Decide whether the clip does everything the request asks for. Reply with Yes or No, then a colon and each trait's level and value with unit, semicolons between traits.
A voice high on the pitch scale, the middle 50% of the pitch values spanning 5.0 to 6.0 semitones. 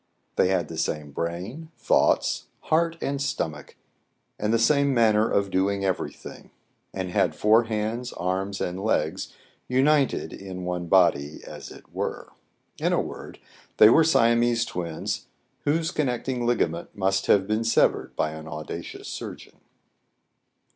No: low, 105 Hz; average, 5.3 semitones